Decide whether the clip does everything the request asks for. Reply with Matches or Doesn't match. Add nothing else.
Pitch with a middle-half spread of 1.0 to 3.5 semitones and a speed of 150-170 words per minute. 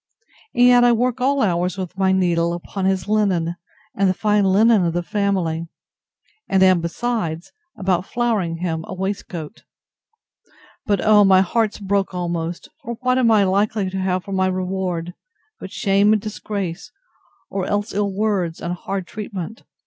Matches